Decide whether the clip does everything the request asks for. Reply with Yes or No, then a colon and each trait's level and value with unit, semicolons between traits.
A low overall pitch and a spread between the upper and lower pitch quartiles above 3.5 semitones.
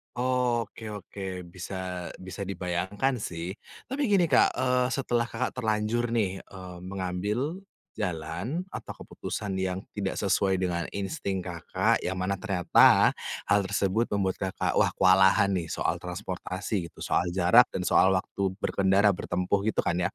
No: very low, 95 Hz; average, 3.0 semitones